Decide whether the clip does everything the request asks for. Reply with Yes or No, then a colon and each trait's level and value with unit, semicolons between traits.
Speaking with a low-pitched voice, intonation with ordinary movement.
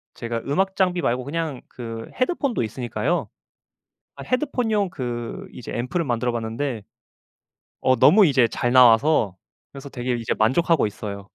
No: low, 130 Hz; wide, 6.5 semitones